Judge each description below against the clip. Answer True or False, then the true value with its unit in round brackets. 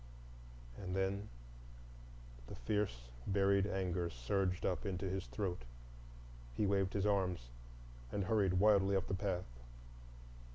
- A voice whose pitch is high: False (95 Hz)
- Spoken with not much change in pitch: True (1.6 semitones)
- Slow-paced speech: True (120 wpm)